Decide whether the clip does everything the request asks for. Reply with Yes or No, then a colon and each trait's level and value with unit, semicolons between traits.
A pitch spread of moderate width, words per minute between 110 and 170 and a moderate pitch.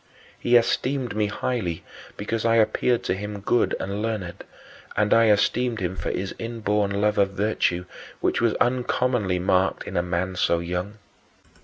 No: average, 3.5 semitones; average, 160 wpm; low, 105 Hz